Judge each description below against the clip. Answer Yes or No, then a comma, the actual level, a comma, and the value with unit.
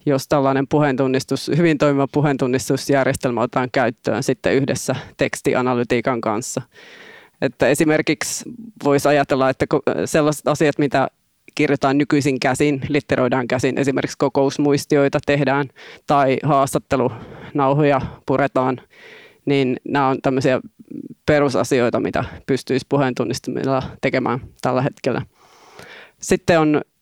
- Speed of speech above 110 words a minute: No, slow, 95 wpm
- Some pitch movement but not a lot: No, narrow, 2.0 semitones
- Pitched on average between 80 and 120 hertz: No, medium, 140 Hz